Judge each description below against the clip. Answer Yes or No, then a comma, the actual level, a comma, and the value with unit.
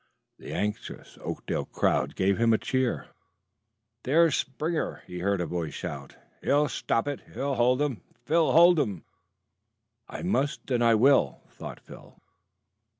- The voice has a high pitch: No, low, 125 Hz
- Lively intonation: Yes, wide, 6.6 semitones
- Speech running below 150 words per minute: Yes, average, 140 wpm